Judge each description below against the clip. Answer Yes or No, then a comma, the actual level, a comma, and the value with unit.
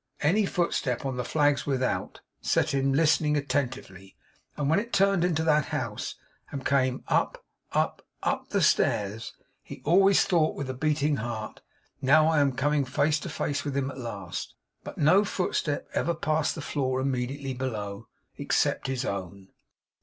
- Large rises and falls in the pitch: No, average, 3.3 semitones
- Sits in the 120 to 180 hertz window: Yes, medium, 140 Hz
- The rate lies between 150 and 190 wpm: Yes, average, 160 wpm